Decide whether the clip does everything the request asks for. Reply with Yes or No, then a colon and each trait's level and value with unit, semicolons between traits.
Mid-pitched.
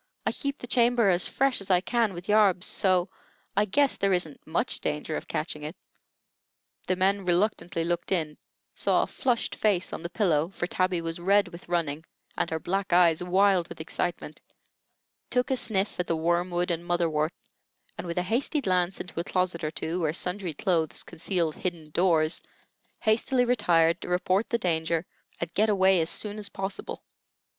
Yes: medium, 180 Hz